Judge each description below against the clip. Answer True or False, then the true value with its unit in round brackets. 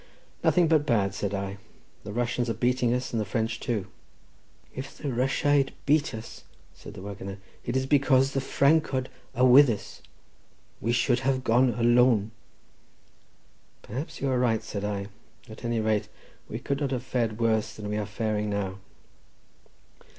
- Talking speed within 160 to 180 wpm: True (165 wpm)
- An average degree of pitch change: True (3.6 semitones)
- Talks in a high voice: False (120 Hz)